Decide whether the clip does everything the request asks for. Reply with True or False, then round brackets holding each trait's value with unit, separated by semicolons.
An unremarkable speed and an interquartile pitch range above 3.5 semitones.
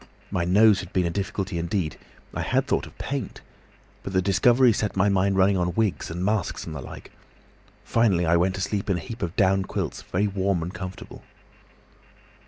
False (190 wpm; 2.4 semitones)